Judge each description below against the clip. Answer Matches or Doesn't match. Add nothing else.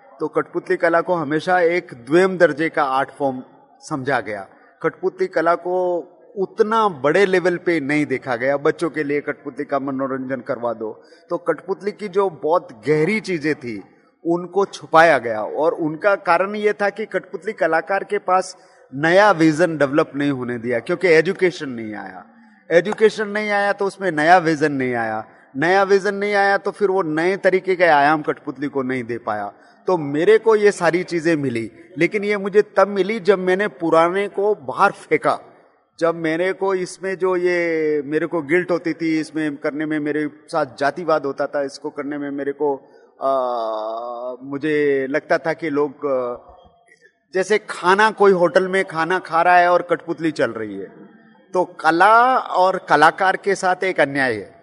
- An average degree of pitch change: Matches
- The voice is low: Doesn't match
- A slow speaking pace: Doesn't match